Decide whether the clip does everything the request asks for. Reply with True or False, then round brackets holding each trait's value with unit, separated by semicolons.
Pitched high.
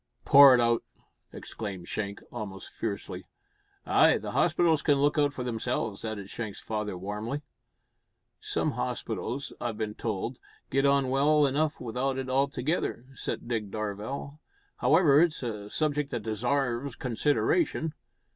False (125 Hz)